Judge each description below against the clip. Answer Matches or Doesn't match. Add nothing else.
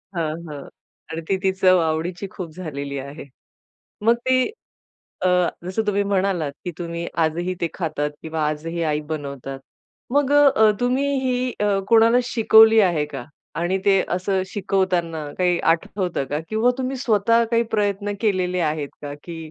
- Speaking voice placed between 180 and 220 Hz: Matches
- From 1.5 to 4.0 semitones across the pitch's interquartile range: Doesn't match